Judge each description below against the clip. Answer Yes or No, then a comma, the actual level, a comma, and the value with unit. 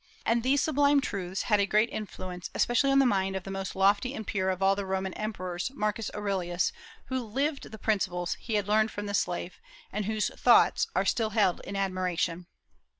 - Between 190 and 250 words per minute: Yes, average, 200 wpm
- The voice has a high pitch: Yes, high, 200 Hz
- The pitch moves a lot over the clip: No, average, 2.8 semitones